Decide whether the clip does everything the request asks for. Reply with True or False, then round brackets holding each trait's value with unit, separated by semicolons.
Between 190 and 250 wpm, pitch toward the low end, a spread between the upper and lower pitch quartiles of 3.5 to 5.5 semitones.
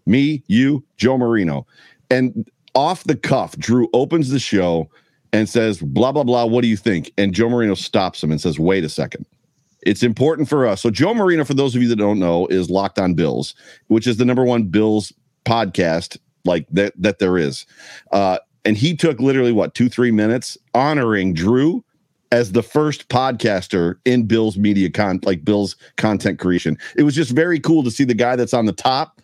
True (200 wpm; 115 Hz; 4.8 semitones)